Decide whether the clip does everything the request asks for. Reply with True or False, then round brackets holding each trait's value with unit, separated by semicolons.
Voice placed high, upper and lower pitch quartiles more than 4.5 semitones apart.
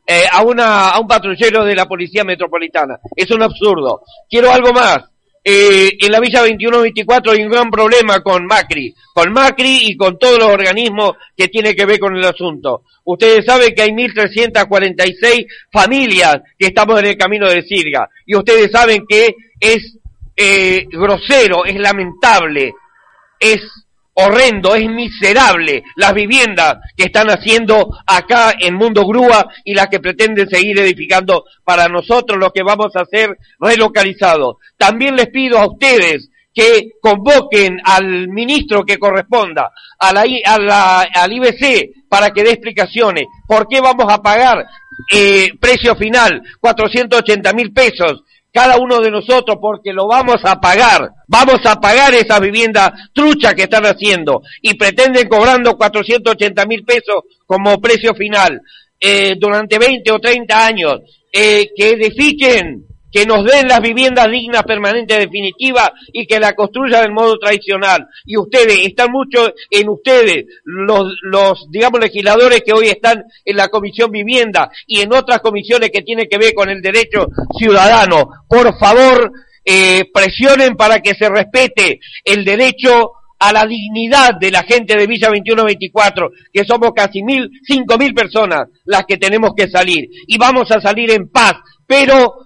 False (215 Hz; 3.2 semitones)